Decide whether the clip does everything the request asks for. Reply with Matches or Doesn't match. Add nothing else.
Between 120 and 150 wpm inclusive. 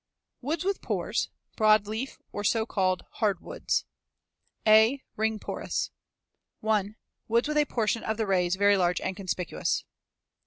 Matches